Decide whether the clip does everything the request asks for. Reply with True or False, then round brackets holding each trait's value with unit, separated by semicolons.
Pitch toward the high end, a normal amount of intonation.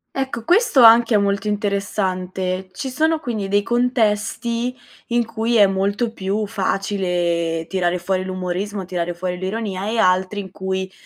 True (200 Hz; 3.5 semitones)